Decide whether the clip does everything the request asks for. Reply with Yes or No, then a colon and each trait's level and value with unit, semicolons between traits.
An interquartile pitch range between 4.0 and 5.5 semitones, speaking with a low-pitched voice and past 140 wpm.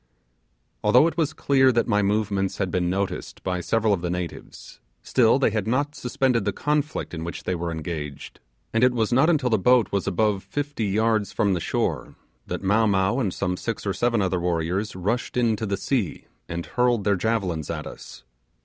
Yes: average, 4.7 semitones; low, 105 Hz; average, 195 wpm